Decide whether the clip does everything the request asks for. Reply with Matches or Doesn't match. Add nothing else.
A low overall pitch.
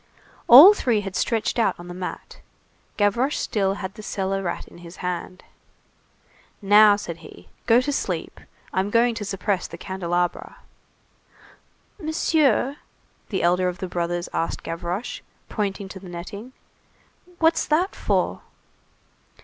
Doesn't match